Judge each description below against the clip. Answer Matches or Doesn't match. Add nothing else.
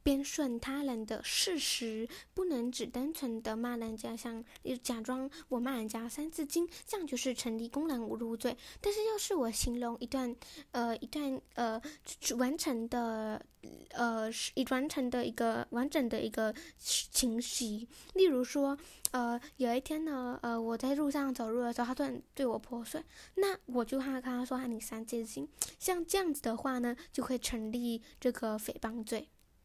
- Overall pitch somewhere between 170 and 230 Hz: Doesn't match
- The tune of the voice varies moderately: Matches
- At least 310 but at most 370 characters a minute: Doesn't match